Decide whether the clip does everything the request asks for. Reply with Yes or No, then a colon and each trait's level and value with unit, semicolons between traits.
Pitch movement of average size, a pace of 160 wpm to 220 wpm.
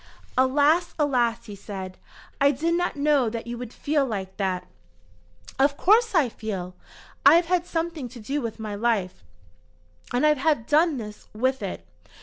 No: wide, 5.9 semitones; average, 165 wpm